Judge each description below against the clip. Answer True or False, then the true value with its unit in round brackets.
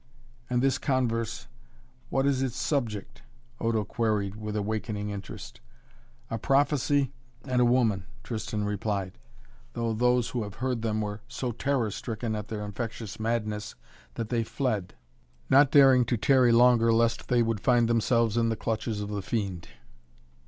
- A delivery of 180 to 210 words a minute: False (150 wpm)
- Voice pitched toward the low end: True (115 Hz)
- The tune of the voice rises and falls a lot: False (2.7 semitones)